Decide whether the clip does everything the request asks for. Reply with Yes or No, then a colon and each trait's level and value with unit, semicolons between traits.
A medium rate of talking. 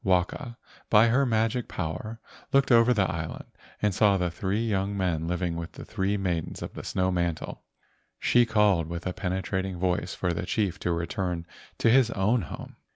Yes: average, 180 wpm